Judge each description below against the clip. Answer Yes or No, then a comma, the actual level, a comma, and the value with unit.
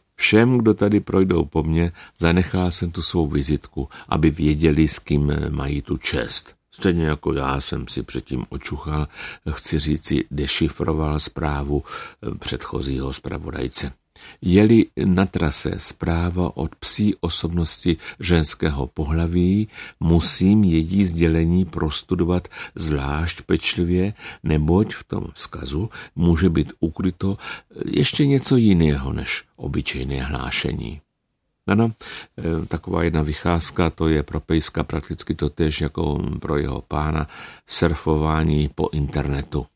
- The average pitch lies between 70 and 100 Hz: Yes, very low, 80 Hz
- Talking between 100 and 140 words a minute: Yes, slow, 115 wpm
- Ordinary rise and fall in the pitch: Yes, average, 3.2 semitones